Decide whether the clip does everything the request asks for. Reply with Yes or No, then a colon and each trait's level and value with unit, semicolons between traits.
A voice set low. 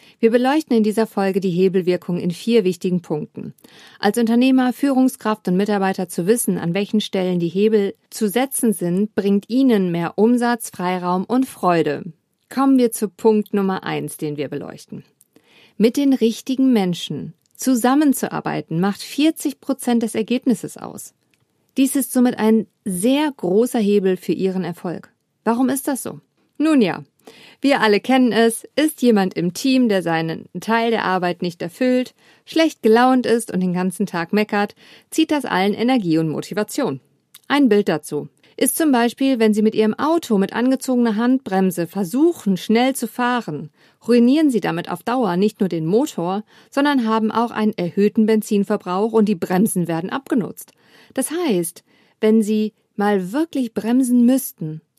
No: high, 215 Hz